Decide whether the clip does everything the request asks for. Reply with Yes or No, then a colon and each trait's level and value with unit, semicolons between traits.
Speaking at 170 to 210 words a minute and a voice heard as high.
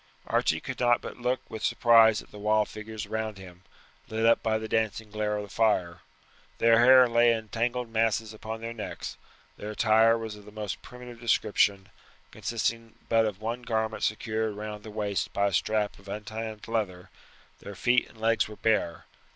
No: average, 185 wpm; low, 110 Hz